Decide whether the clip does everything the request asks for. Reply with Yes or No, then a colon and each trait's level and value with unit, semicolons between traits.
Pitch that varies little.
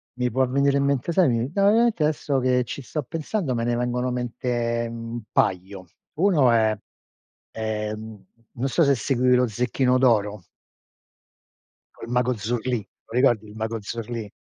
No: average, 3.0 semitones